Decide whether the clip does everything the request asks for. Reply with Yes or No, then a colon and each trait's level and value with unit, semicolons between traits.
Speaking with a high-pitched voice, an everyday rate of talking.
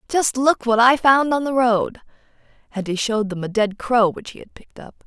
No: high, 235 Hz; fast, 225 wpm